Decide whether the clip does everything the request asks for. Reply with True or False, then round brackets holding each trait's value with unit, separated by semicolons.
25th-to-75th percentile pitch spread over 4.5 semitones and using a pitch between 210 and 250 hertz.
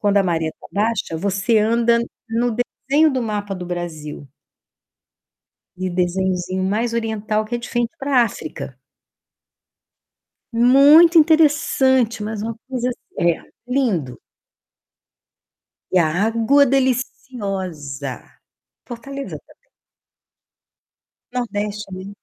True (5.0 semitones; 220 Hz)